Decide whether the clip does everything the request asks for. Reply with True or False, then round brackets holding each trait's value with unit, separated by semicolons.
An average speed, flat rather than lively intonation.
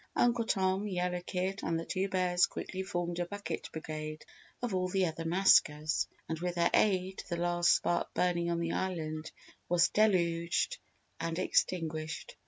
True (160 wpm; 2.1 semitones)